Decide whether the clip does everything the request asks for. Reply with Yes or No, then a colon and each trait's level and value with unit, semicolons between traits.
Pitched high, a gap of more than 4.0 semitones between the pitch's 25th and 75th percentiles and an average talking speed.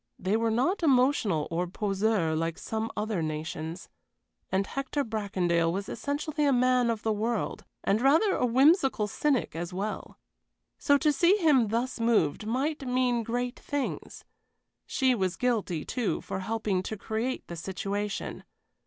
Yes: high, 225 Hz; average, 5.2 semitones; average, 150 wpm